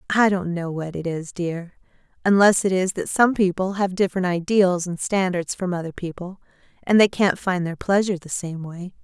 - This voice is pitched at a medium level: Yes, medium, 180 Hz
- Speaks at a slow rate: No, average, 200 wpm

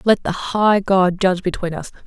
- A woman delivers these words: Yes, female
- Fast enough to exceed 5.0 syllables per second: No, 4.9 syllables/s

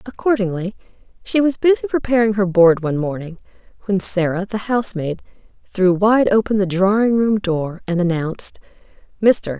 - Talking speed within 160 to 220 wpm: No, average, 145 wpm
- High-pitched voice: Yes, high, 200 Hz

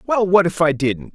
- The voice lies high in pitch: No, medium, 170 Hz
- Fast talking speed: Yes, fast, 260 wpm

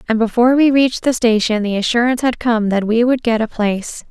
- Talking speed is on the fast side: Yes, fast, 235 wpm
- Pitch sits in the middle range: No, high, 230 Hz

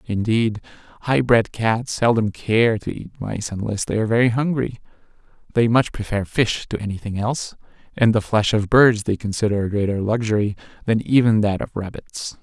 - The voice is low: Yes, low, 110 Hz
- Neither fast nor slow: Yes, average, 175 wpm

